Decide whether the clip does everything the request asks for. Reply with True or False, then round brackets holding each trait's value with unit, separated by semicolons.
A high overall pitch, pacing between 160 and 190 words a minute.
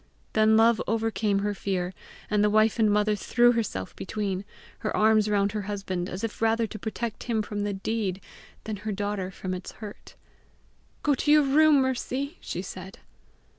True (210 Hz; 175 wpm)